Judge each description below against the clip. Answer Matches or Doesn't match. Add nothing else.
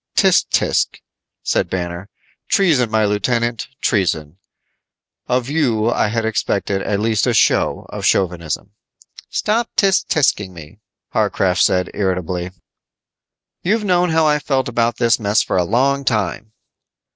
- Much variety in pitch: Matches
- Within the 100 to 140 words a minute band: Matches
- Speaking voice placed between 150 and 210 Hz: Doesn't match